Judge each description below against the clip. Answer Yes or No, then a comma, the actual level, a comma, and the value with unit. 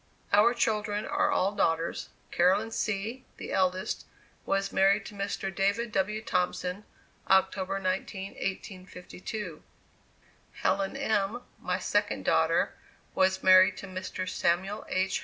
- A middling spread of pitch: No, narrow, 2.1 semitones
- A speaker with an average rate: No, slow, 120 wpm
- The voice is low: No, high, 195 Hz